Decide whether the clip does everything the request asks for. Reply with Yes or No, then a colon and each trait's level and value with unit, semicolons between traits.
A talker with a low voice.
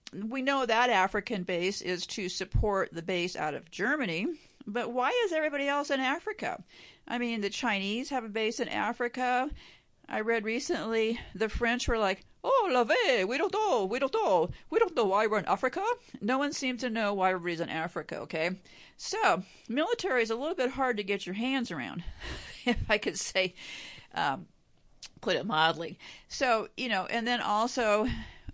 No: high, 235 Hz